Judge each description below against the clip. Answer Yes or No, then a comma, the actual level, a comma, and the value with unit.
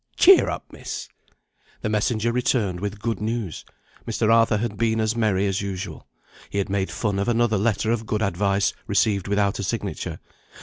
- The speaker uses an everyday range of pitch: No, narrow, 2.3 semitones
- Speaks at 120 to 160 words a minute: No, average, 175 wpm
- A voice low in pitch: Yes, low, 105 Hz